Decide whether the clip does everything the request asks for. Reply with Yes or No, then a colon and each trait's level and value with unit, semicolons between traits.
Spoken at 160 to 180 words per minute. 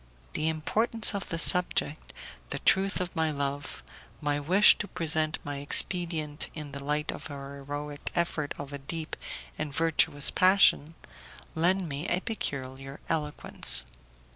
No: average, 140 wpm